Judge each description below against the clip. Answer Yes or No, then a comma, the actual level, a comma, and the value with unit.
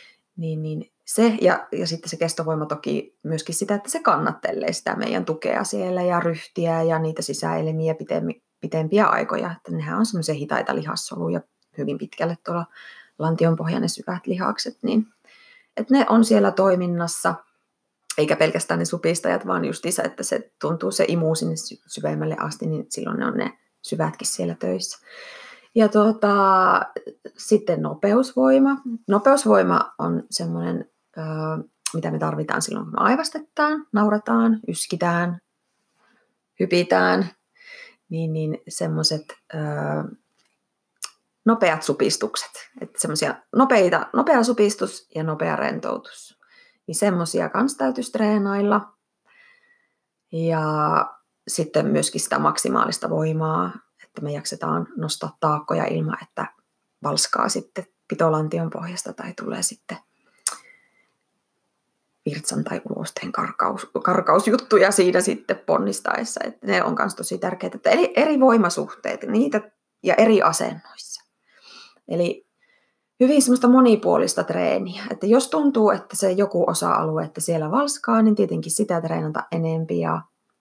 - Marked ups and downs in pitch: Yes, wide, 7.0 semitones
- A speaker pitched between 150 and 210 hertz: Yes, medium, 185 Hz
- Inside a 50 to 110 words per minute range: No, average, 120 wpm